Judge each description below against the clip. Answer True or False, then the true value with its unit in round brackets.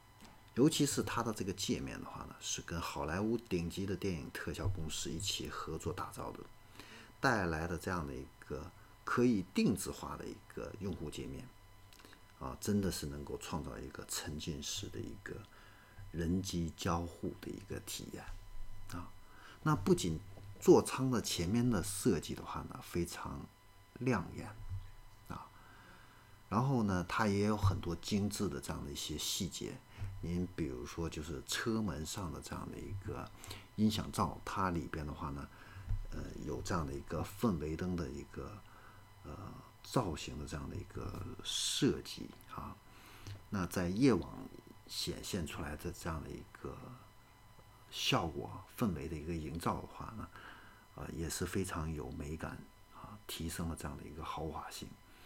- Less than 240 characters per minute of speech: True (230 characters per minute)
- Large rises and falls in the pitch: False (4.2 semitones)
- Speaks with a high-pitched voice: False (95 Hz)